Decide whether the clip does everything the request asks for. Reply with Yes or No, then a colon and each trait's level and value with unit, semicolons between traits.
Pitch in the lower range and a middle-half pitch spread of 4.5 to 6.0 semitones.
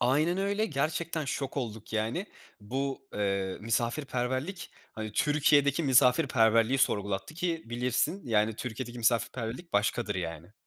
Yes: low, 125 Hz; average, 5.1 semitones